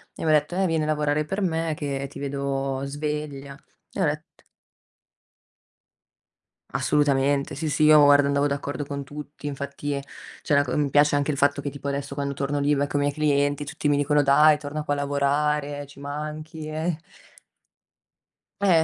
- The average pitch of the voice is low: No, medium, 145 Hz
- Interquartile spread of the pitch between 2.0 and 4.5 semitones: No, narrow, 1.2 semitones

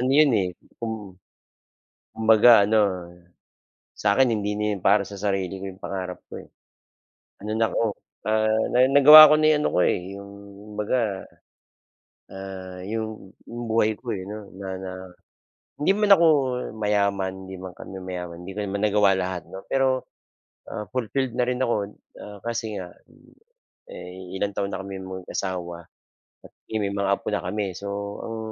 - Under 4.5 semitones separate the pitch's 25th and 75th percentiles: Yes, average, 2.9 semitones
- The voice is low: Yes, low, 100 Hz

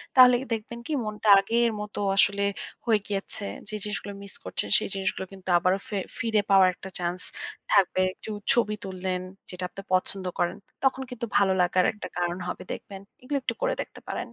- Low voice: No, high, 200 Hz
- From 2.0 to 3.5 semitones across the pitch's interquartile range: Yes, average, 2.9 semitones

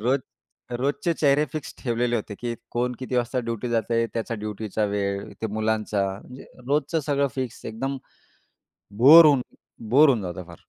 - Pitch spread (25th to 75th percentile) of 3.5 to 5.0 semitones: Yes, average, 4.0 semitones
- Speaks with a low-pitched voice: Yes, low, 120 Hz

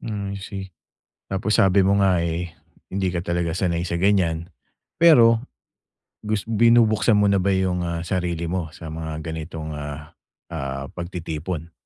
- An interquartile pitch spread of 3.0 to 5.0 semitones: Yes, average, 3.3 semitones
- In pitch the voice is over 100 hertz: No, very low, 90 Hz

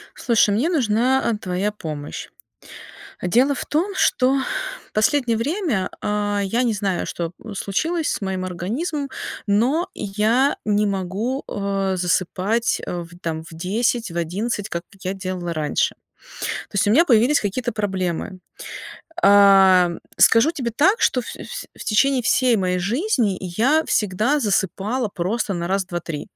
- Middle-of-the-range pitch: No, high, 210 Hz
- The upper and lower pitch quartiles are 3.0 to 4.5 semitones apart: No, average, 5.3 semitones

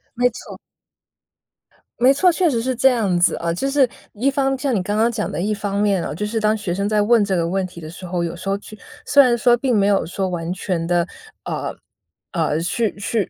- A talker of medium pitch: No, high, 205 Hz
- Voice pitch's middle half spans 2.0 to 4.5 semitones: No, average, 5.1 semitones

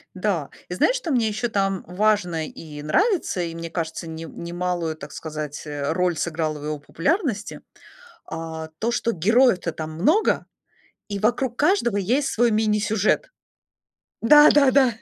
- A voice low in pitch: No, medium, 185 Hz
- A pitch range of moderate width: No, wide, 6.6 semitones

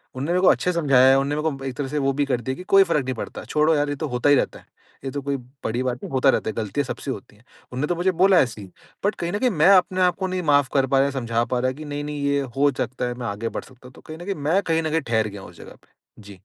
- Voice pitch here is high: No, medium, 140 Hz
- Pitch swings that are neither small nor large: Yes, average, 4.1 semitones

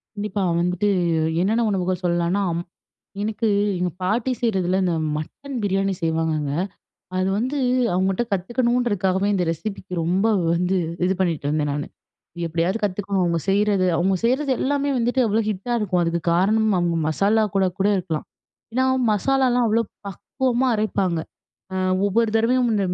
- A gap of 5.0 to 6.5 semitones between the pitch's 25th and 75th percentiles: No, average, 4.1 semitones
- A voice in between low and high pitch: No, high, 195 Hz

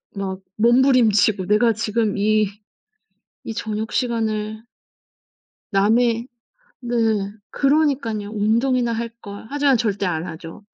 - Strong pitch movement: No, narrow, 2.5 semitones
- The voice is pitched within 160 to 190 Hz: No, high, 220 Hz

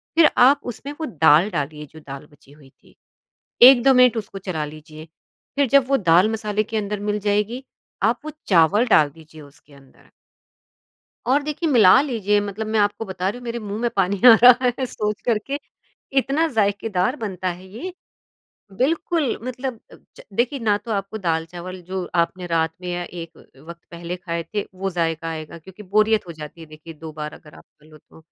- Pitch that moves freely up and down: Yes, wide, 6.3 semitones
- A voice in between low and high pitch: No, high, 200 Hz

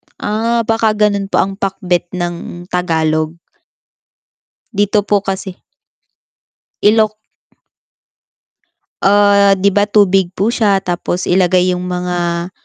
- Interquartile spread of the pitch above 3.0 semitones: No, narrow, 2.5 semitones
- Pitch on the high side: Yes, high, 195 Hz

